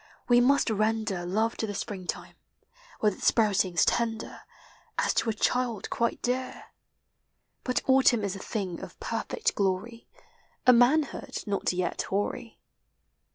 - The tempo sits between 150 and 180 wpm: No, average, 140 wpm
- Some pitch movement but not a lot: Yes, average, 3.7 semitones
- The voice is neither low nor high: No, high, 225 Hz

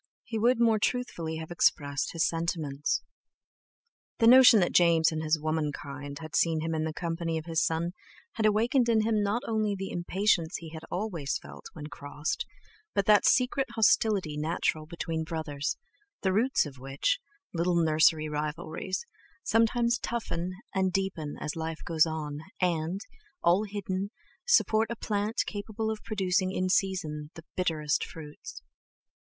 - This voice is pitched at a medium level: Yes, medium, 175 Hz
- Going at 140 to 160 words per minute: Yes, average, 145 wpm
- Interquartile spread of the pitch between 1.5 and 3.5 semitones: No, average, 5.2 semitones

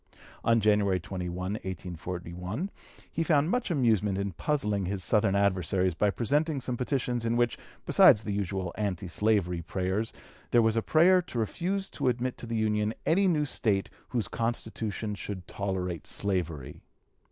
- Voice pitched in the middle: No, low, 105 Hz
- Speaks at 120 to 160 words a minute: Yes, average, 155 wpm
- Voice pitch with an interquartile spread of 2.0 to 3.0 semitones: No, average, 4.6 semitones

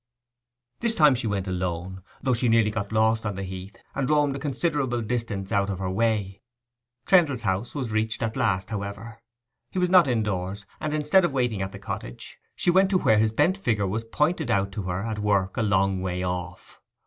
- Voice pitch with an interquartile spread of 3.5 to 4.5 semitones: No, average, 5.2 semitones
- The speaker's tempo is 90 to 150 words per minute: No, fast, 205 wpm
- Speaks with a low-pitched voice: Yes, low, 110 Hz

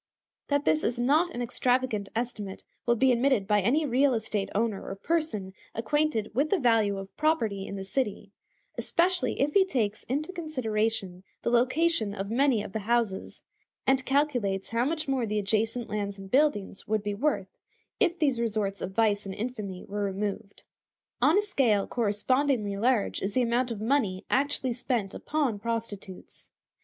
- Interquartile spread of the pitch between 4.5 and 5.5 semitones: Yes, average, 5.0 semitones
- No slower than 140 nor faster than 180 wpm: Yes, average, 170 wpm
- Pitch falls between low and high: No, high, 230 Hz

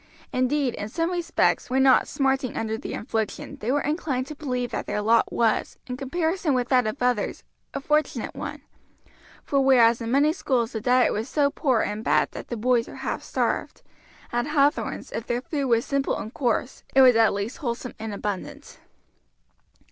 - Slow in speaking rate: No, average, 185 wpm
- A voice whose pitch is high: Yes, very high, 250 Hz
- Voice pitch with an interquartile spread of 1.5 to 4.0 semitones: Yes, average, 3.4 semitones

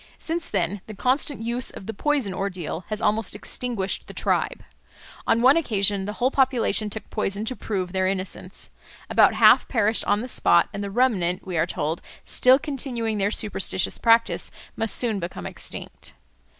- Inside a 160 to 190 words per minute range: Yes, average, 170 wpm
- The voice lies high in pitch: Yes, high, 215 Hz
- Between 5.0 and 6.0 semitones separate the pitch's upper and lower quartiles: No, average, 4.2 semitones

